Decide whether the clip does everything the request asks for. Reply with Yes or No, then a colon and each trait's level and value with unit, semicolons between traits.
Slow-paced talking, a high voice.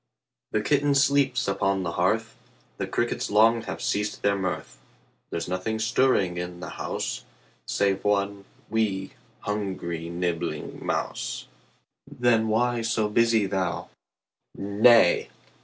No: slow, 125 wpm; low, 100 Hz